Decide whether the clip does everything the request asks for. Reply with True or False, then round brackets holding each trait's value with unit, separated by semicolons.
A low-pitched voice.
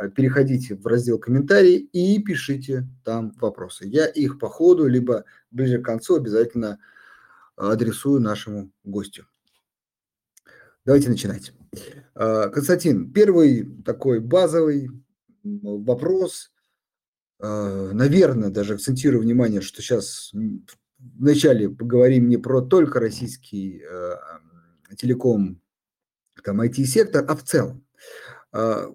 True (125 Hz)